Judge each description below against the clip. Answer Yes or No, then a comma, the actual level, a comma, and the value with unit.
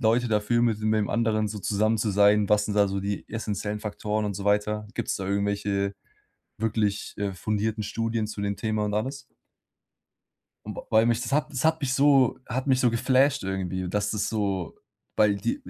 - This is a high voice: No, low, 105 Hz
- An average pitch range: No, narrow, 2.1 semitones